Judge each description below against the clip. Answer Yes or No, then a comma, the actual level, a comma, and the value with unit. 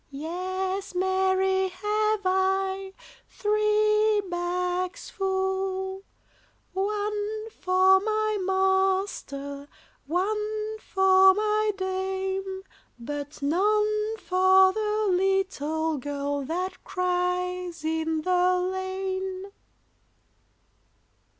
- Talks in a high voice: Yes, very high, 380 Hz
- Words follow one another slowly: Yes, slow, 75 wpm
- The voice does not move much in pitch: Yes, narrow, 2.0 semitones